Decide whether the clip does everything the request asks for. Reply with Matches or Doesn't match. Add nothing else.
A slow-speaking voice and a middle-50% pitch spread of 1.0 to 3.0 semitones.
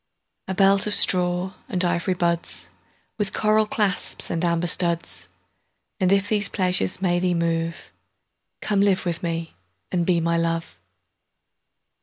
Matches